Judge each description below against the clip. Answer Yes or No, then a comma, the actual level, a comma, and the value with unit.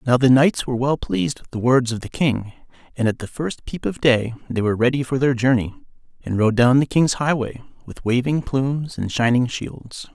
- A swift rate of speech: Yes, fast, 220 wpm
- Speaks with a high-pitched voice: No, low, 125 Hz